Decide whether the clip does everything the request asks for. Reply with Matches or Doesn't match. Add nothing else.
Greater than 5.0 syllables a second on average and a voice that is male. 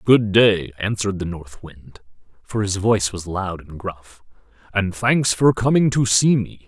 Doesn't match